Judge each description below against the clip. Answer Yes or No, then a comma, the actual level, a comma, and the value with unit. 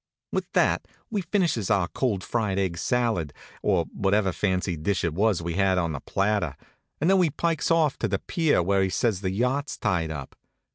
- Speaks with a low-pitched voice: Yes, low, 100 Hz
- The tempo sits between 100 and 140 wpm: No, average, 195 wpm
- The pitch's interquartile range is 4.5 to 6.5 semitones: Yes, wide, 5.6 semitones